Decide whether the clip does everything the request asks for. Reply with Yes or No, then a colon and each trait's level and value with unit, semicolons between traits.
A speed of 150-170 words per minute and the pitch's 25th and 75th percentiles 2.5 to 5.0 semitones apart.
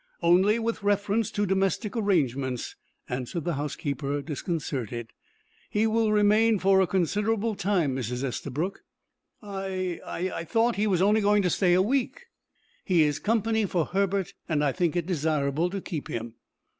No: average, 155 wpm; wide, 5.5 semitones